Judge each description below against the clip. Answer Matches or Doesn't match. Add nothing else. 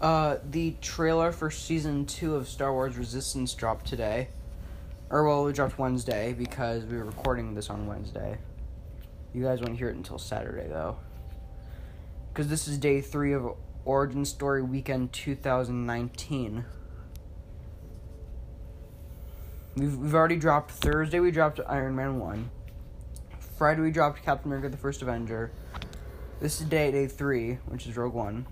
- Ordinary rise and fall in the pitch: Doesn't match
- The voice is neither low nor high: Doesn't match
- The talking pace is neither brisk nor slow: Matches